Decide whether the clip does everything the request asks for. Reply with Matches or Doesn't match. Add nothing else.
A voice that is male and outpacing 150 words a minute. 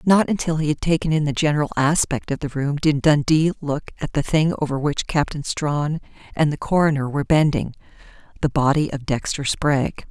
Doesn't match